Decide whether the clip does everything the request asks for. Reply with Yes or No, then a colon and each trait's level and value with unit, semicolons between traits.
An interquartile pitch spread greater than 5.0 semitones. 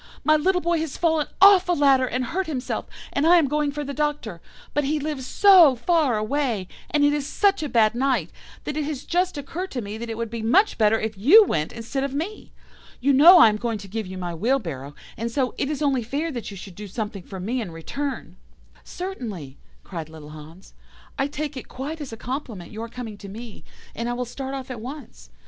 Yes: wide, 5.6 semitones